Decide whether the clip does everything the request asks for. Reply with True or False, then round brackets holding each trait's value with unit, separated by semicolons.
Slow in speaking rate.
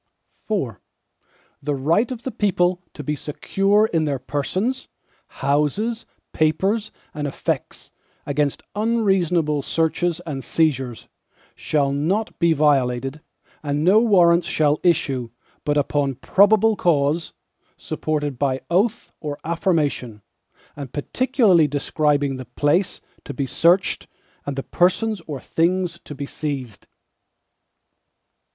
True (115 wpm)